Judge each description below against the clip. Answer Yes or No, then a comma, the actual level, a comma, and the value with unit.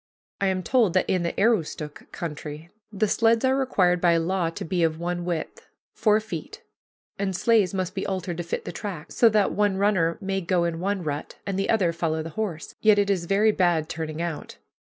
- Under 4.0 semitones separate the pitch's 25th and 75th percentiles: Yes, average, 3.5 semitones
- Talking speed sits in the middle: No, fast, 210 wpm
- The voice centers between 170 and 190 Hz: Yes, medium, 185 Hz